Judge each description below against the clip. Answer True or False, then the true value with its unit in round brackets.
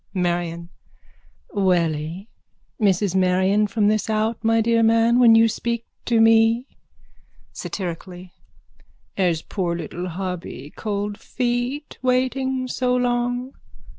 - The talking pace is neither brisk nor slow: False (105 wpm)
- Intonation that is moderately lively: True (4.6 semitones)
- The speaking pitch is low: False (215 Hz)